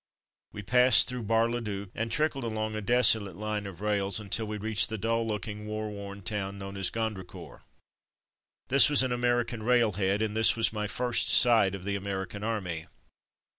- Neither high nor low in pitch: No, low, 110 Hz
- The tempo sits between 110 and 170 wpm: No, average, 180 wpm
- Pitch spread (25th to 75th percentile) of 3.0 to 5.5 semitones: No, narrow, 2.4 semitones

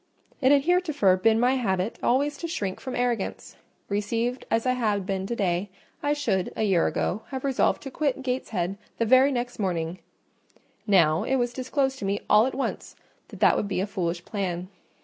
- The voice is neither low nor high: No, high, 225 Hz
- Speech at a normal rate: Yes, average, 190 wpm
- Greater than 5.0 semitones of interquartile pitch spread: Yes, wide, 5.4 semitones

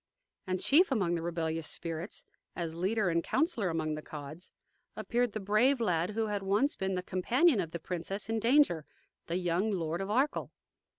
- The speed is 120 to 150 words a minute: No, average, 180 wpm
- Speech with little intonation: No, average, 5.0 semitones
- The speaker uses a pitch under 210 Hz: Yes, high, 190 Hz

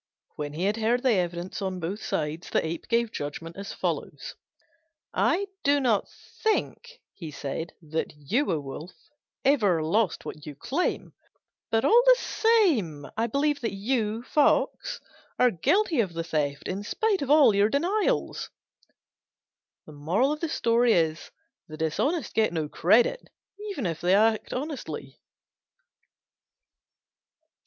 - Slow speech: Yes, slow, 130 wpm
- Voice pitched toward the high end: Yes, high, 215 Hz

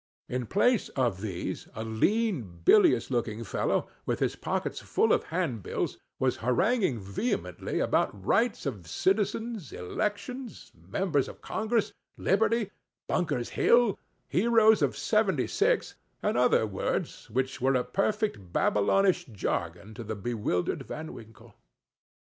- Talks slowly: Yes, slow, 110 wpm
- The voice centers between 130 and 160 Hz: Yes, low, 135 Hz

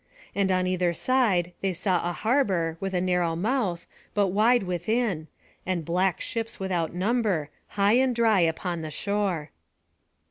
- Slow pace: No, average, 150 wpm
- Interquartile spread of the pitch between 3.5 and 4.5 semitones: Yes, average, 3.8 semitones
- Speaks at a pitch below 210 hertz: Yes, medium, 185 Hz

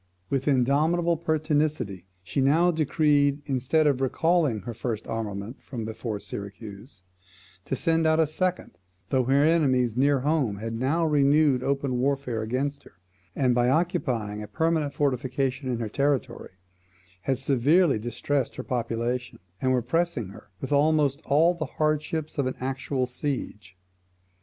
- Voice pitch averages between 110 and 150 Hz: Yes, low, 135 Hz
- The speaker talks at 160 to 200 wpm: No, average, 145 wpm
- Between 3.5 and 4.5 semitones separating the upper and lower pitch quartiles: Yes, average, 4.1 semitones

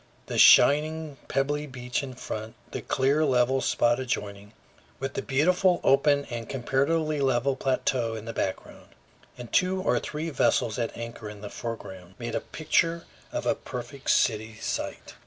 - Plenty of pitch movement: No, average, 4.2 semitones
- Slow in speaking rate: No, average, 155 wpm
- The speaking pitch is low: Yes, low, 130 Hz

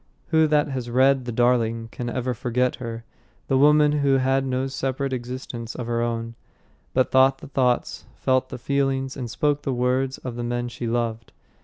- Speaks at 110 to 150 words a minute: No, average, 185 wpm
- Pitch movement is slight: Yes, narrow, 2.0 semitones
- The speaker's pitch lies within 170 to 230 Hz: No, low, 130 Hz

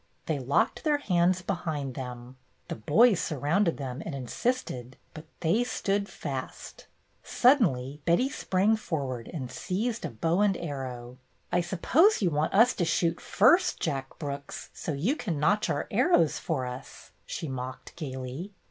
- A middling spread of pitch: No, wide, 6.9 semitones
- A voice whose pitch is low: No, medium, 160 Hz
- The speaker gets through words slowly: No, average, 150 wpm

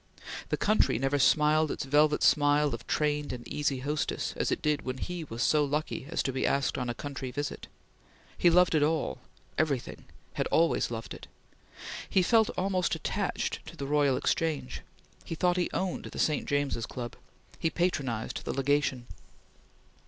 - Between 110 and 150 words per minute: No, average, 170 wpm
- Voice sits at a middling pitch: Yes, medium, 145 Hz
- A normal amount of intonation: Yes, average, 3.2 semitones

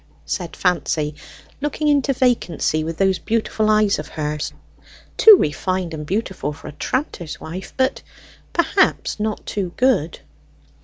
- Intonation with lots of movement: Yes, wide, 8.1 semitones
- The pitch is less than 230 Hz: Yes, high, 190 Hz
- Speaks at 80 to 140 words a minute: Yes, slow, 135 wpm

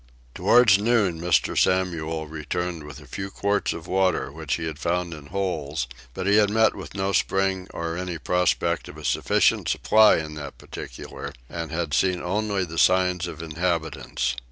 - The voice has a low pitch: Yes, very low, 90 Hz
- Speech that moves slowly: No, average, 175 wpm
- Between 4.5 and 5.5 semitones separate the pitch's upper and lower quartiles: No, average, 3.3 semitones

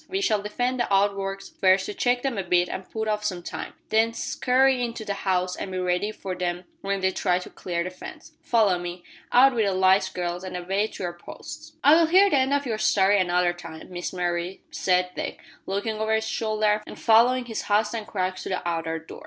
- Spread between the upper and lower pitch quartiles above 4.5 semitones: No, average, 3.7 semitones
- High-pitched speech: Yes, high, 195 Hz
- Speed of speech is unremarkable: No, fast, 225 wpm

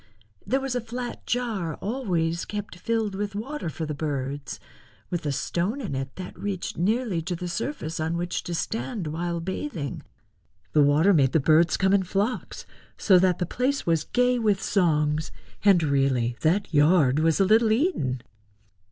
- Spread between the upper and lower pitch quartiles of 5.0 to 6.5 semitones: Yes, wide, 5.6 semitones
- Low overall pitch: No, medium, 175 Hz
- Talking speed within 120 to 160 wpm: No, average, 170 wpm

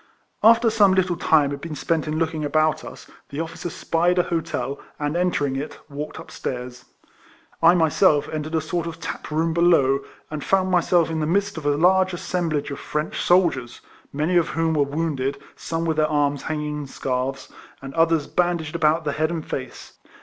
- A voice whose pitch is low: No, medium, 160 Hz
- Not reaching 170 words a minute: No, average, 185 wpm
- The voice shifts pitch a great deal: No, average, 2.8 semitones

